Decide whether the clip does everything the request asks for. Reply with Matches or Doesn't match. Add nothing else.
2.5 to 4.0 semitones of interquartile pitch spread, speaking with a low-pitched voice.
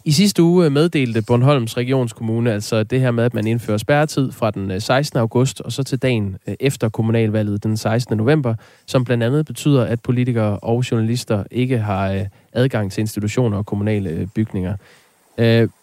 Matches